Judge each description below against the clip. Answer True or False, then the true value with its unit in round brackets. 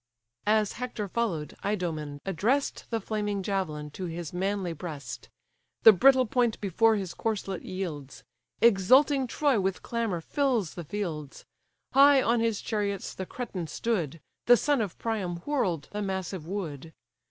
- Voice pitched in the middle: False (200 Hz)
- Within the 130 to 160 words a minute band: True (140 wpm)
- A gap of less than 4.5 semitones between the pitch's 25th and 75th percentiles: False (5.0 semitones)